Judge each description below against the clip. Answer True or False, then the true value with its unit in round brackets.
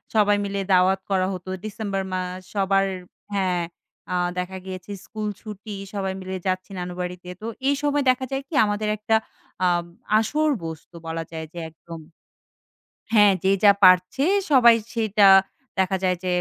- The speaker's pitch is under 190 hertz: False (195 Hz)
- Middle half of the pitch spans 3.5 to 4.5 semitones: False (2.7 semitones)